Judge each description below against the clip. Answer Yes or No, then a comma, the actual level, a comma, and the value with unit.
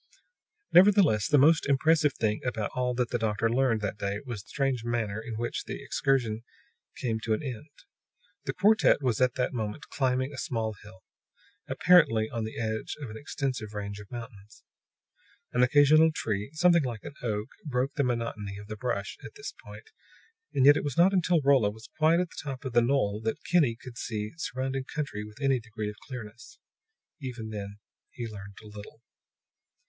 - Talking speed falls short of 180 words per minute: No, average, 185 wpm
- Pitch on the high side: No, low, 120 Hz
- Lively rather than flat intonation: No, average, 4.4 semitones